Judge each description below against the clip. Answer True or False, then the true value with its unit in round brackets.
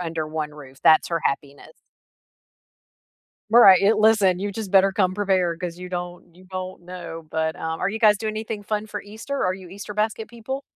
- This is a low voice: False (185 Hz)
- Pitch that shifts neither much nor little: True (3.8 semitones)